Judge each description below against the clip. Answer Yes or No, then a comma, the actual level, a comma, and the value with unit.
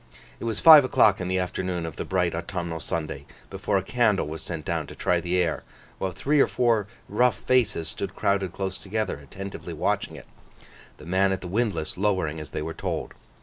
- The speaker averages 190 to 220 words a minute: Yes, average, 200 wpm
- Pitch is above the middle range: No, very low, 95 Hz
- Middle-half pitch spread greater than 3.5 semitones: Yes, average, 3.9 semitones